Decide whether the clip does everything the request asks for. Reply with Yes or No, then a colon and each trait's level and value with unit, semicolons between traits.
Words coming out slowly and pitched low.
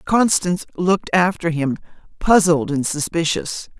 No: slow, 110 wpm; medium, 170 Hz